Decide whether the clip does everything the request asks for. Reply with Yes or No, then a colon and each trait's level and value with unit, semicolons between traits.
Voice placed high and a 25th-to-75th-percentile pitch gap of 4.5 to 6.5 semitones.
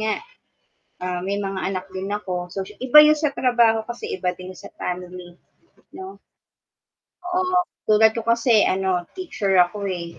Yes: high, 200 Hz; average, 4.8 semitones